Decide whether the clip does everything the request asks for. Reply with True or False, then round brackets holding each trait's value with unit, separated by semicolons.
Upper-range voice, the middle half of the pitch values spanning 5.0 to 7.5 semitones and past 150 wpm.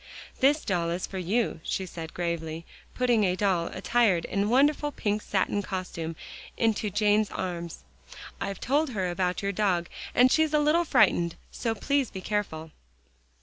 True (200 Hz; 5.3 semitones; 160 wpm)